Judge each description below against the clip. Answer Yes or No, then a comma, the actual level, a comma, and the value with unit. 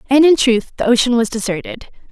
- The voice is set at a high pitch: Yes, high, 240 Hz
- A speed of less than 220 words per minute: Yes, average, 200 wpm